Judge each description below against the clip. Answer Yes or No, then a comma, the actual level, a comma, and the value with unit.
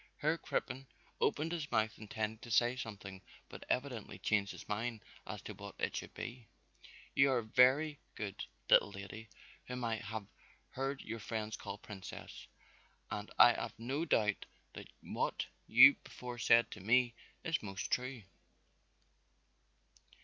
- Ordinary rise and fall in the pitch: Yes, average, 3.1 semitones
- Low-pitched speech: Yes, low, 115 Hz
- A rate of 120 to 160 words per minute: Yes, average, 145 wpm